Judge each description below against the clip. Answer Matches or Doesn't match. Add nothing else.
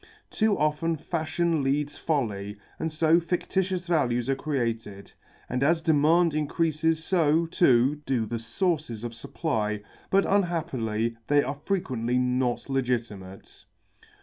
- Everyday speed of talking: Doesn't match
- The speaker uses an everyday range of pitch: Doesn't match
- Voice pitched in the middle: Matches